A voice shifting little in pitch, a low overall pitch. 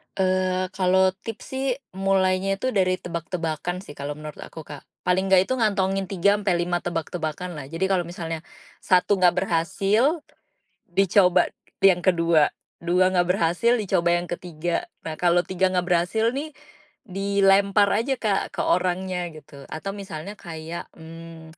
No: narrow, 2.3 semitones; medium, 185 Hz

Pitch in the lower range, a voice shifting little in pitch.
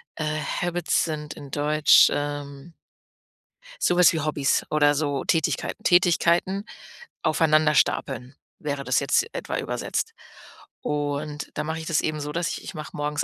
No: medium, 150 Hz; narrow, 1.7 semitones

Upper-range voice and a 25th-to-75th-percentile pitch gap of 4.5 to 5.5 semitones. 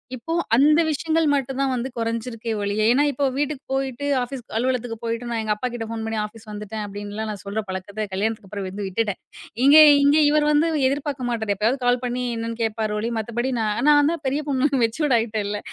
No: high, 230 Hz; average, 3.8 semitones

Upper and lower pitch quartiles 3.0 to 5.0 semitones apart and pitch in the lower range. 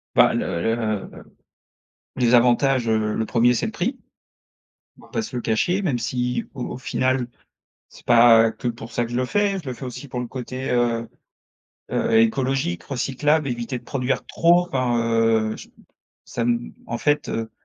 No: narrow, 2.5 semitones; low, 120 Hz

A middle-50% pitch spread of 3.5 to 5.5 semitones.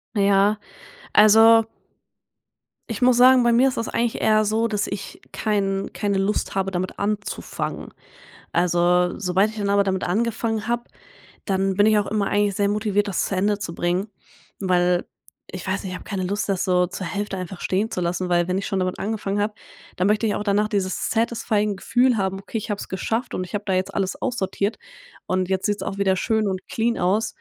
No: narrow, 2.5 semitones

